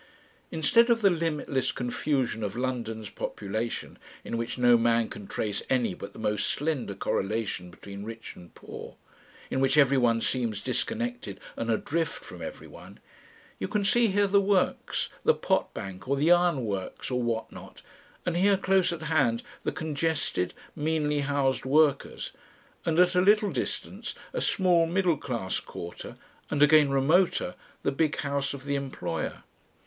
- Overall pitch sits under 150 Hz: Yes, medium, 140 Hz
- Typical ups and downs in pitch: No, wide, 6.5 semitones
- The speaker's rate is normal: Yes, average, 155 wpm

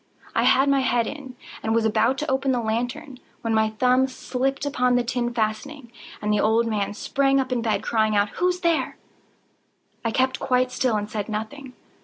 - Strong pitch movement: No, average, 3.4 semitones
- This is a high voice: Yes, high, 245 Hz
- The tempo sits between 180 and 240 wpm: Yes, average, 190 wpm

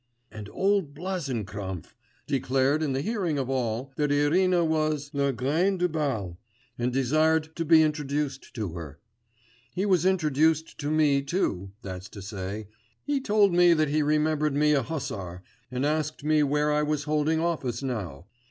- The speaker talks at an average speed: Yes, average, 160 wpm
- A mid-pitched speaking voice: Yes, medium, 150 Hz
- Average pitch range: Yes, average, 4.0 semitones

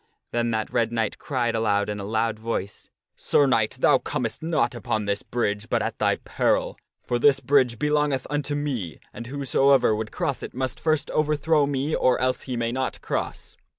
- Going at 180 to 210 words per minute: Yes, average, 190 wpm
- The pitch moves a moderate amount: Yes, average, 4.2 semitones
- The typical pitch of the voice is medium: No, low, 125 Hz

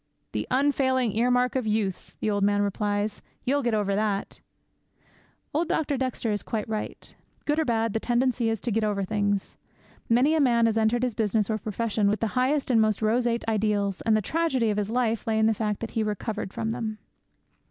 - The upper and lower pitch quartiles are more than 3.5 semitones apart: No, average, 2.8 semitones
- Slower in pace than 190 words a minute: No, fast, 205 wpm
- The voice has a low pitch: No, high, 225 Hz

